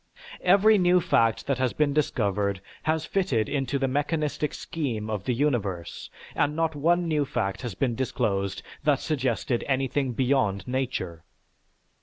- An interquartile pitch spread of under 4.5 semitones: No, wide, 5.6 semitones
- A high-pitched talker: No, low, 135 Hz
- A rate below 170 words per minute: Yes, average, 145 wpm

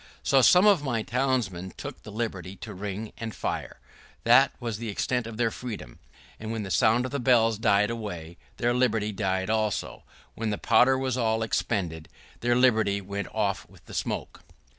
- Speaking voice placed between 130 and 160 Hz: No, low, 110 Hz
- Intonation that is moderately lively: Yes, average, 3.2 semitones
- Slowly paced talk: No, average, 185 wpm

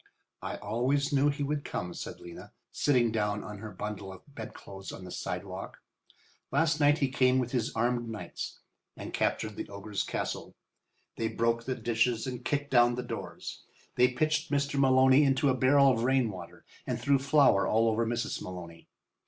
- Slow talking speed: No, average, 175 wpm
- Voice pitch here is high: No, low, 120 Hz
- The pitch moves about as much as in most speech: Yes, average, 4.1 semitones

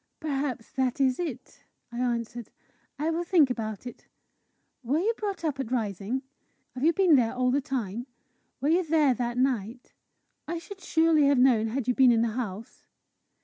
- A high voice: Yes, very high, 260 Hz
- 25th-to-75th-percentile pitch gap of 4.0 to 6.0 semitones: Yes, average, 4.4 semitones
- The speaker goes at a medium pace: Yes, average, 180 wpm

